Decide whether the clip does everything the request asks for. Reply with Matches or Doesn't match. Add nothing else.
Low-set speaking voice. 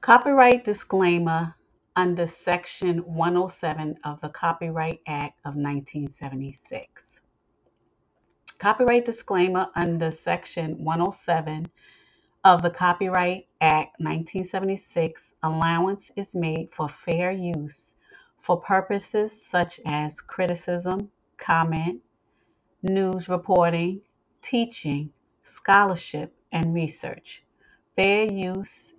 Doesn't match